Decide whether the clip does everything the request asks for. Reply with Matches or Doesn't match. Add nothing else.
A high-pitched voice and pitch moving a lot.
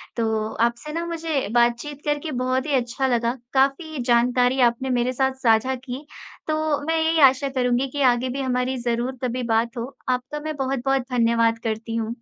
Doesn't match